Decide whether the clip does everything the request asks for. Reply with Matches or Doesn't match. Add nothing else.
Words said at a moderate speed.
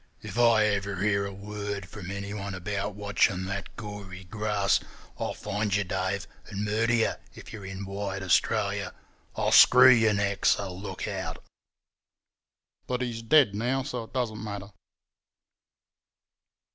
Matches